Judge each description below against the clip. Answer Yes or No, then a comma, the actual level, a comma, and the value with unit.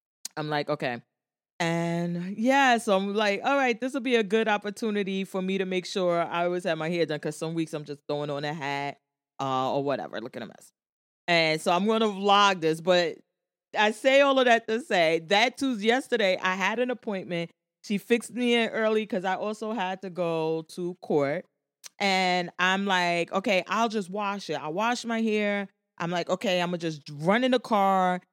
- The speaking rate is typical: No, fast, 210 wpm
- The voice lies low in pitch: No, medium, 185 Hz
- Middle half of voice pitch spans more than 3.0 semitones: Yes, average, 4.7 semitones